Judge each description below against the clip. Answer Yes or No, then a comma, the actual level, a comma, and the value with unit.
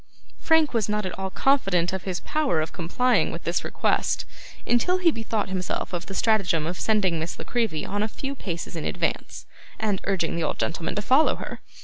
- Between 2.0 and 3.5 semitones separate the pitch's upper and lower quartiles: No, wide, 5.4 semitones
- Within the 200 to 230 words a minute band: Yes, fast, 205 wpm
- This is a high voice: Yes, high, 195 Hz